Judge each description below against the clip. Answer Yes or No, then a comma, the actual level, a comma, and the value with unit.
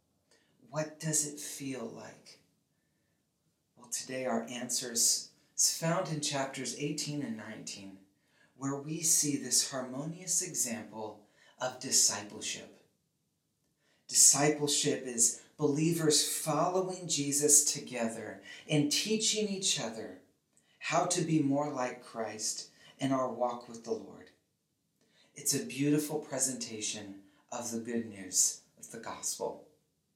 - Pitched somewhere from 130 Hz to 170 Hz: Yes, medium, 140 Hz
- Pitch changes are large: No, average, 4.3 semitones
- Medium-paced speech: No, slow, 115 wpm